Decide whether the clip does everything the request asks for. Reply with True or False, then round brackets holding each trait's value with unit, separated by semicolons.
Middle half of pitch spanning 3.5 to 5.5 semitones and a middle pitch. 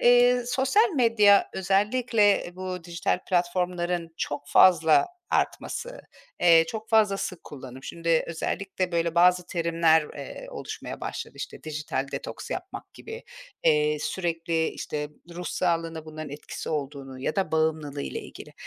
True (3.9 semitones; 170 Hz)